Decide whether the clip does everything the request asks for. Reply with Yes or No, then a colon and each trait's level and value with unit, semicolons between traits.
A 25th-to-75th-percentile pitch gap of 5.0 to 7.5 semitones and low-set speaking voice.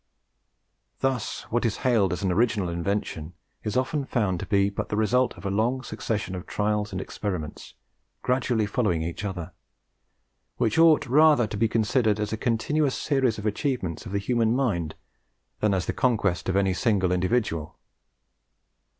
No: average, 4.5 semitones; low, 105 Hz